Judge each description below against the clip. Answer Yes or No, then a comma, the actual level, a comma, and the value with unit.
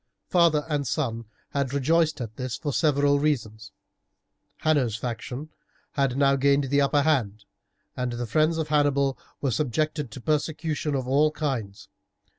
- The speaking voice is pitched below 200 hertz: Yes, medium, 140 Hz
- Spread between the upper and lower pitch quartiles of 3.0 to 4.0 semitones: Yes, average, 3.3 semitones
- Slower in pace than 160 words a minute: Yes, average, 145 wpm